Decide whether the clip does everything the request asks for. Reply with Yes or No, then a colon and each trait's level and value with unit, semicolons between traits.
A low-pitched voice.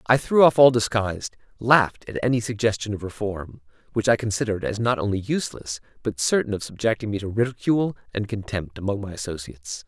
Yes: low, 105 Hz